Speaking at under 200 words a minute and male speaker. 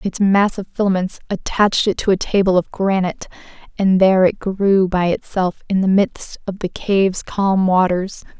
No: average, 180 wpm; female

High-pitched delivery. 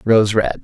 No: low, 110 Hz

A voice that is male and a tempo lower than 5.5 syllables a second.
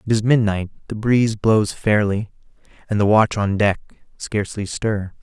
Yes: male; 4.5 syllables/s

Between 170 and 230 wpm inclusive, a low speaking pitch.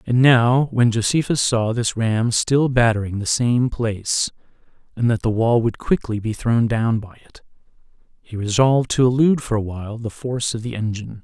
Yes: average, 185 wpm; low, 115 Hz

